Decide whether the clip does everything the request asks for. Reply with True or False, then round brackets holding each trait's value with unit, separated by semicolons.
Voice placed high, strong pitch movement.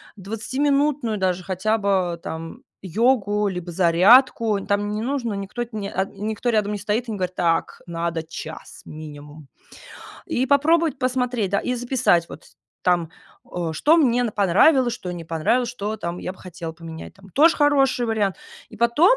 True (205 Hz; 5.8 semitones)